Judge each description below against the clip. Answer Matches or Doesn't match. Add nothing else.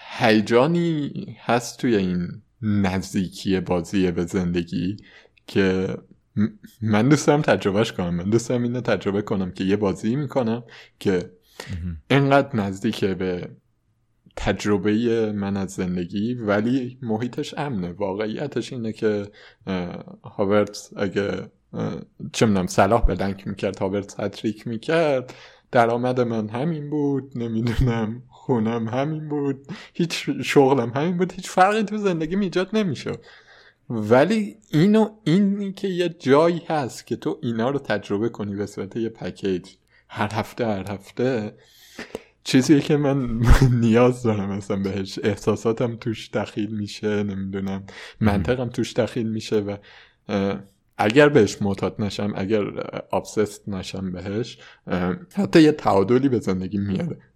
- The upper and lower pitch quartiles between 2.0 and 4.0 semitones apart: Doesn't match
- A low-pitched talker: Matches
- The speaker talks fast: Doesn't match